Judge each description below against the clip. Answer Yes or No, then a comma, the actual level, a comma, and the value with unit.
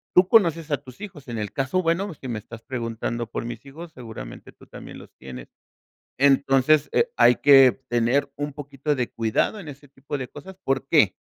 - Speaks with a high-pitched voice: No, low, 135 Hz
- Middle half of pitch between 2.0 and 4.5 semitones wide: Yes, average, 4.0 semitones